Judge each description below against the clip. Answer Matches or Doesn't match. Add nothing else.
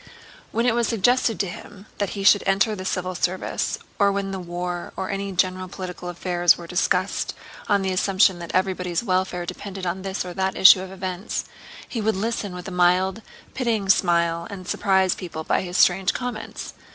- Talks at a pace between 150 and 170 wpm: Doesn't match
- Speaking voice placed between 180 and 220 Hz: Matches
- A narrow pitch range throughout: Matches